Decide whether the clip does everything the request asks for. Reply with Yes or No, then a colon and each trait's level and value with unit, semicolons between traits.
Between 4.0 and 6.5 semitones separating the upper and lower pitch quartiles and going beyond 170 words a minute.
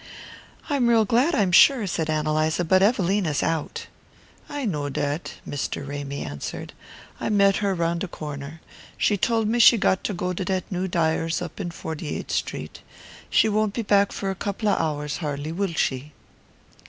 Yes: average, 5.0 semitones; average, 180 wpm